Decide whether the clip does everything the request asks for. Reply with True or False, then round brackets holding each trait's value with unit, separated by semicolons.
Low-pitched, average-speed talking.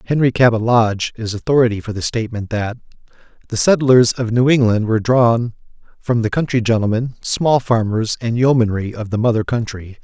True (115 Hz; 165 wpm)